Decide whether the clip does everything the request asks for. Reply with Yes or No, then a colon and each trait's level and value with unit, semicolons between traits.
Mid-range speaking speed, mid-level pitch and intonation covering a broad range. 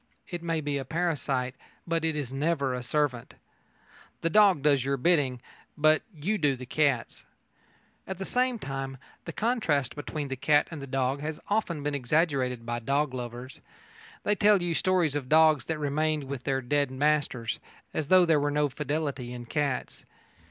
No: average, 175 wpm; medium, 145 Hz; average, 3.3 semitones